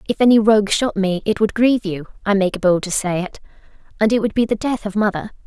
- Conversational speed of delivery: No, fast, 250 wpm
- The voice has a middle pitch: No, high, 205 Hz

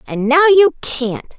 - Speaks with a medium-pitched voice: No, very high, 290 Hz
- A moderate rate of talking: Yes, average, 175 wpm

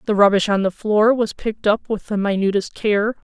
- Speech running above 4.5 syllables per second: Yes, 5.2 syllables/s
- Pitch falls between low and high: No, high, 210 Hz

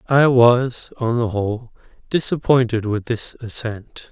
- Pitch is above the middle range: No, low, 120 Hz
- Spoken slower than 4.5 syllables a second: Yes, 3.9 syllables/s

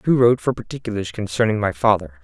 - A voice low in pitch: Yes, low, 105 Hz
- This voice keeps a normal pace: Yes, average, 190 wpm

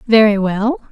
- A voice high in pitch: Yes, high, 220 Hz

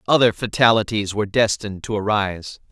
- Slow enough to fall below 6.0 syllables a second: No, 6.1 syllables/s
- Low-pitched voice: Yes, low, 105 Hz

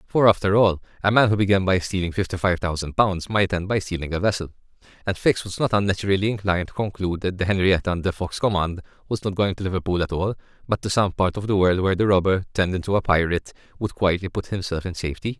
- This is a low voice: Yes, very low, 95 Hz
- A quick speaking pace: Yes, fast, 235 wpm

